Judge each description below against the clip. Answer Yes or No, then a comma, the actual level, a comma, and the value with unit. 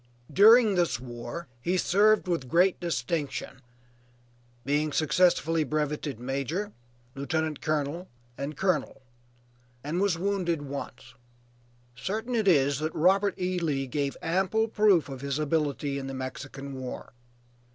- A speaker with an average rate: No, slow, 125 wpm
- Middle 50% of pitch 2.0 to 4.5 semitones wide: No, average, 4.9 semitones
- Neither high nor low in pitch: Yes, medium, 155 Hz